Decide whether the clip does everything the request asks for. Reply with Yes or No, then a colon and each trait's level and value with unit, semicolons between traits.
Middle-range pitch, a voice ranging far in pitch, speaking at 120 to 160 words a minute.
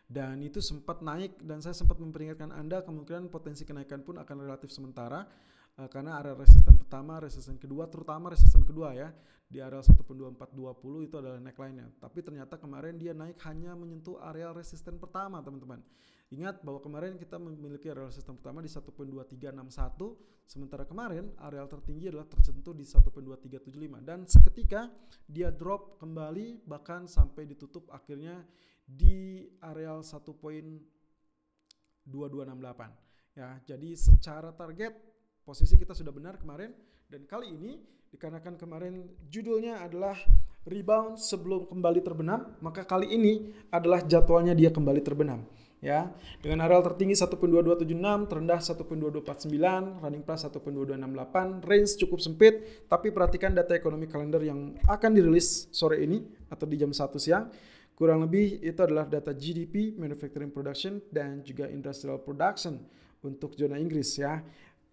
No: medium, 160 Hz; average, 3.9 semitones; average, 135 wpm